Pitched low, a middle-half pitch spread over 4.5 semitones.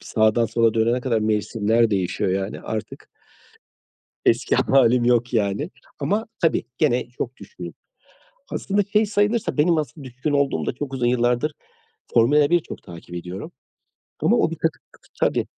Yes: low, 120 Hz; average, 5.3 semitones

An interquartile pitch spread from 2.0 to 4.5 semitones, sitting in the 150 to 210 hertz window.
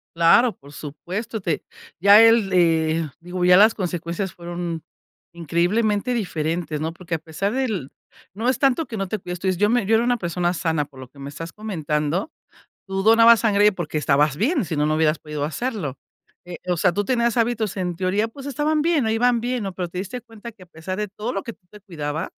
No: wide, 5.4 semitones; medium, 185 Hz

